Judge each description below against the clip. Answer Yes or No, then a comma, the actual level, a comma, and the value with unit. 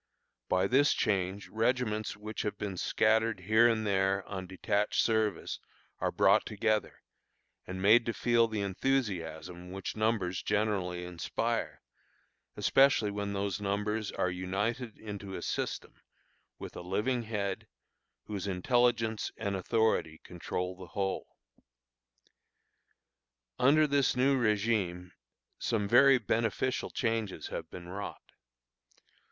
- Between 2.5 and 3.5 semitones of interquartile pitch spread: Yes, average, 3.2 semitones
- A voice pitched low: Yes, low, 105 Hz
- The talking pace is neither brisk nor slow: No, slow, 120 wpm